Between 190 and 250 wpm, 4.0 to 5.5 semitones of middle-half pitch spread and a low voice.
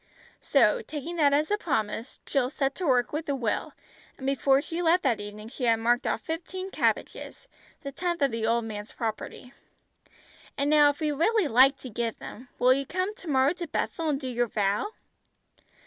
No: average, 195 wpm; average, 5.2 semitones; very high, 275 Hz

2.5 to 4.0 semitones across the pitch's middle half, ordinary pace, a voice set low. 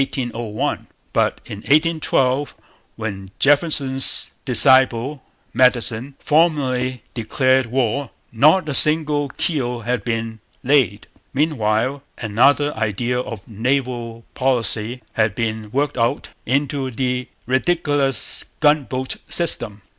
No: average, 3.7 semitones; slow, 95 wpm; low, 130 Hz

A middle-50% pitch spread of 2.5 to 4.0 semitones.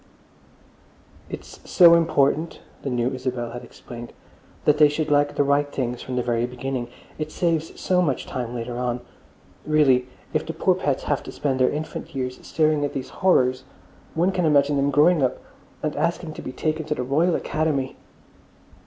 Yes: average, 3.6 semitones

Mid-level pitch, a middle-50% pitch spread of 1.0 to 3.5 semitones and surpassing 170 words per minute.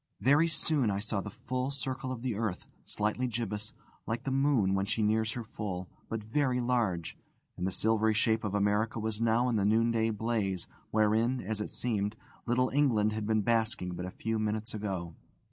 No: low, 110 Hz; narrow, 2.5 semitones; average, 190 wpm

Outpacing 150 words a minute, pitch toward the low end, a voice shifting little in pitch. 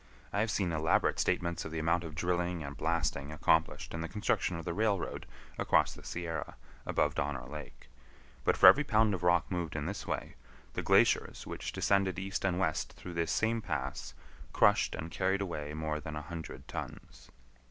No: average, 185 wpm; very low, 85 Hz; average, 3.4 semitones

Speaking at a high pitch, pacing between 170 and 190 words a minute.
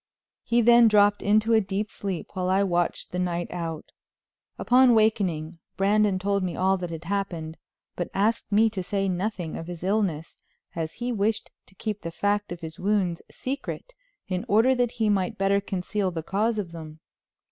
Yes: high, 195 Hz; average, 180 wpm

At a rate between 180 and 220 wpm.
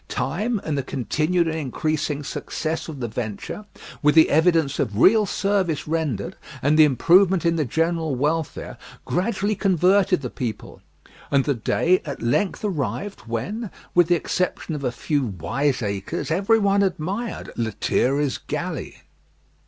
No: average, 145 wpm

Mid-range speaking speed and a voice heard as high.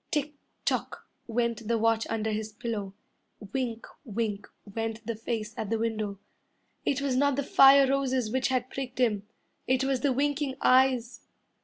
Yes: average, 160 wpm; high, 235 Hz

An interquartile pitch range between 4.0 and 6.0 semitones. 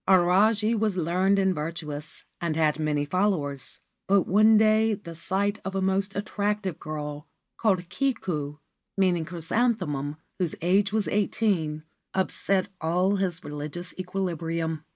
Yes: average, 4.3 semitones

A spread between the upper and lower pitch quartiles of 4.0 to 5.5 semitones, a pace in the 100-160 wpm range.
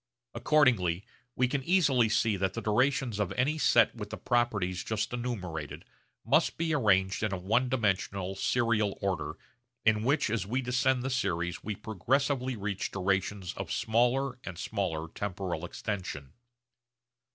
Yes: average, 4.9 semitones; average, 145 wpm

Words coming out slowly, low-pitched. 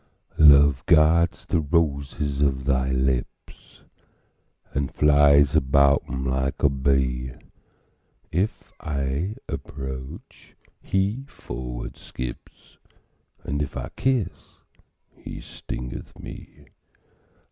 Yes: slow, 90 wpm; very low, 70 Hz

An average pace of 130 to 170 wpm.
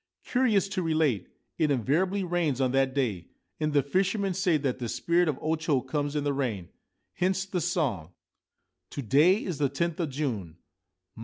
No: average, 180 wpm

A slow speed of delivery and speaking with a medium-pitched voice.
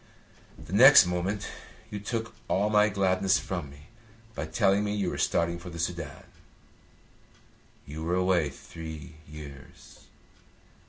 No: slow, 130 wpm; very low, 90 Hz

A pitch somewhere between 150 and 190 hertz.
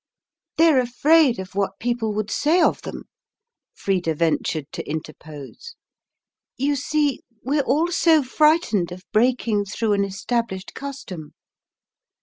No: high, 230 Hz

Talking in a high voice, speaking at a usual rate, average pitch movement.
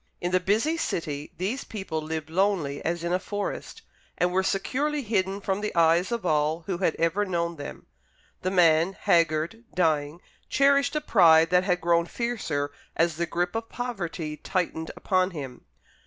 No: medium, 175 Hz; average, 170 wpm; average, 3.7 semitones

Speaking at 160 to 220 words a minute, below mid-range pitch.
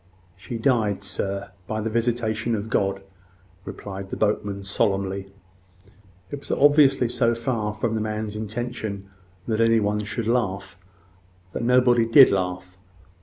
No: slow, 135 wpm; low, 110 Hz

